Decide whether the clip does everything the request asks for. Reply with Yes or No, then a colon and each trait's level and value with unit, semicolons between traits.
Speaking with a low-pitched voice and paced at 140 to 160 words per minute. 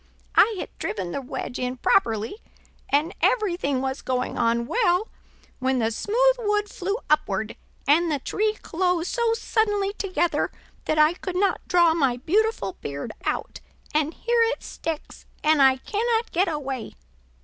No: very high, 330 Hz; average, 150 wpm